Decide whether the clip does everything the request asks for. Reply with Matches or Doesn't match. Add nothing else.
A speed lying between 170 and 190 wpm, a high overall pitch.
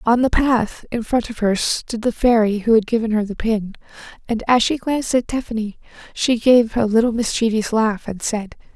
Doesn't match